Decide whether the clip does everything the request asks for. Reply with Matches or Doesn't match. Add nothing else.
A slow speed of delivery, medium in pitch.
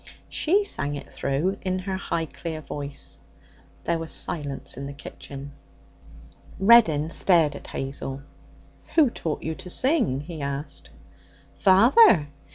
Matches